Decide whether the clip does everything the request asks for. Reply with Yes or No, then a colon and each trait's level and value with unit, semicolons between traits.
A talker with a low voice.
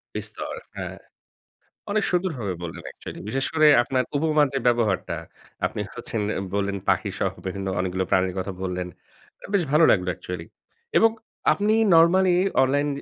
Yes: low, 120 Hz